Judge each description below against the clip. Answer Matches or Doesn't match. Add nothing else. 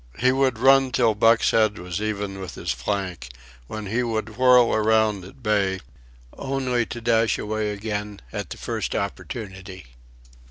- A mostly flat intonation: Doesn't match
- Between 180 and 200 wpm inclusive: Doesn't match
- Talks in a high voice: Doesn't match